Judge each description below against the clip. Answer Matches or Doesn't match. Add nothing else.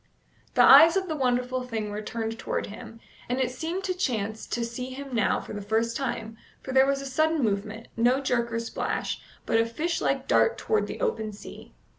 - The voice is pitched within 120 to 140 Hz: Doesn't match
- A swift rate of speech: Matches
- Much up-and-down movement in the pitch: Doesn't match